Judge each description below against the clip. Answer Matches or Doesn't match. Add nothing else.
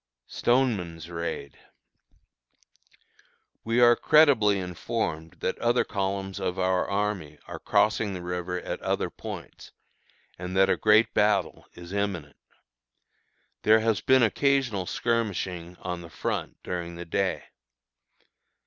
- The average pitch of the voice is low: Matches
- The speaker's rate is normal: Doesn't match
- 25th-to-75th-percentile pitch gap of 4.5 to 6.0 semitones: Doesn't match